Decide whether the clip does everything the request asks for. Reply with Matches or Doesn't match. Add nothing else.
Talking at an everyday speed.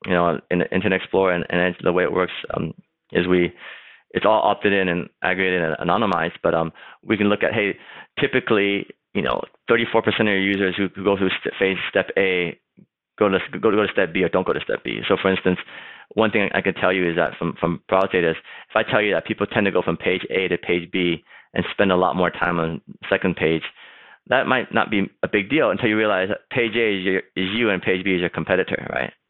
Doesn't match